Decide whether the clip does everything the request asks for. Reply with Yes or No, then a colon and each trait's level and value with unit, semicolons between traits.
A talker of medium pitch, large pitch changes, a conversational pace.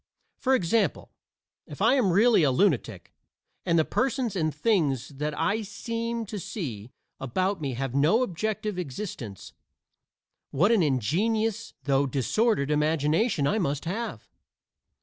No: medium, 175 Hz; wide, 7.5 semitones; slow, 130 wpm